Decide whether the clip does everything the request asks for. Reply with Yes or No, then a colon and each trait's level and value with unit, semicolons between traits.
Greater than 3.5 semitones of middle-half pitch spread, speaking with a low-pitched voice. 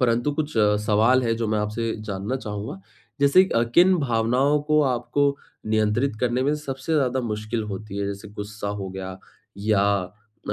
Yes: average, 4.4 semitones; low, 115 Hz